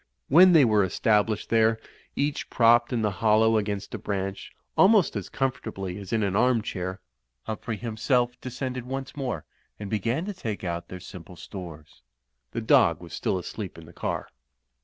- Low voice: Yes, low, 110 Hz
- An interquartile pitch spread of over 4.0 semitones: Yes, average, 4.5 semitones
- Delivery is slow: No, average, 170 wpm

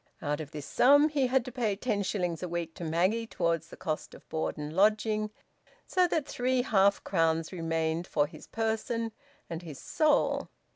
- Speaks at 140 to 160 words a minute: No, average, 185 wpm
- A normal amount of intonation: No, wide, 6.0 semitones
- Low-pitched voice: No, high, 190 Hz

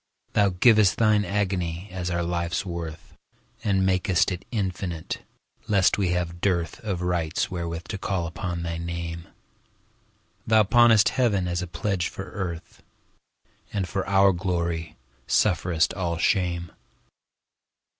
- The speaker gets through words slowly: Yes, slow, 115 wpm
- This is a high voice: No, very low, 90 Hz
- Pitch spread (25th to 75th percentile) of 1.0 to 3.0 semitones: Yes, narrow, 2.5 semitones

